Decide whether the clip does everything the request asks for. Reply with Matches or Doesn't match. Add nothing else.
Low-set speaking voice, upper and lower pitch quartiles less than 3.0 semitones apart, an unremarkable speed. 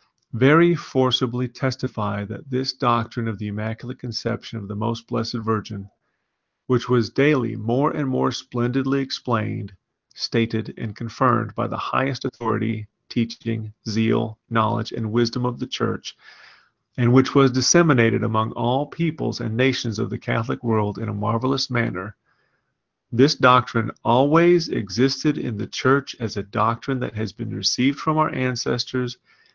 Matches